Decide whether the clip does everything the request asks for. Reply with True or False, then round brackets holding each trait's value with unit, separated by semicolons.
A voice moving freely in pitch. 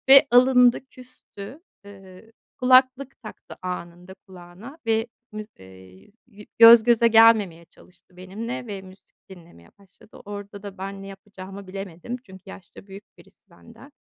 False (3.8 semitones)